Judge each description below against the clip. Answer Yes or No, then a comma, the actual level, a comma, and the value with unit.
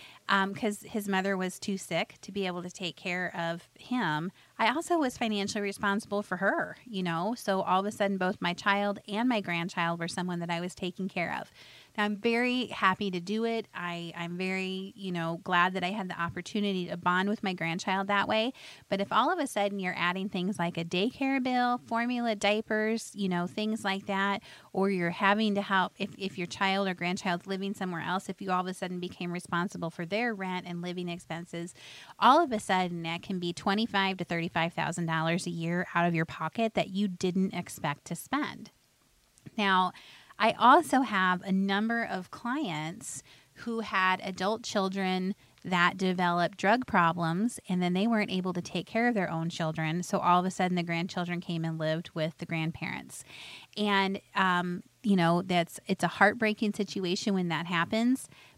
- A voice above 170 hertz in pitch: Yes, high, 190 Hz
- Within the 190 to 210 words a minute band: Yes, average, 200 wpm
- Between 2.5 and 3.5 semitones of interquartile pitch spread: Yes, average, 2.9 semitones